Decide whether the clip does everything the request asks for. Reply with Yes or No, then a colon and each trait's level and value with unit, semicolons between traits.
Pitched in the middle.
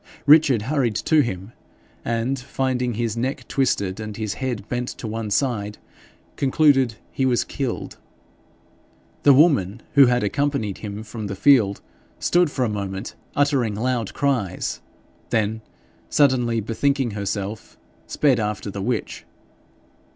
No: low, 120 Hz